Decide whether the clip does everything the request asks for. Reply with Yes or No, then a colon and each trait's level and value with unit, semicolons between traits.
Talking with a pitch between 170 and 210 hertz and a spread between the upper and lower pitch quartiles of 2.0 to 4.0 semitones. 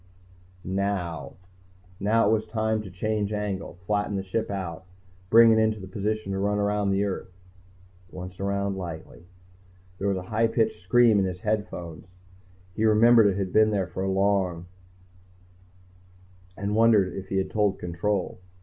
No: low, 100 Hz; narrow, 2.4 semitones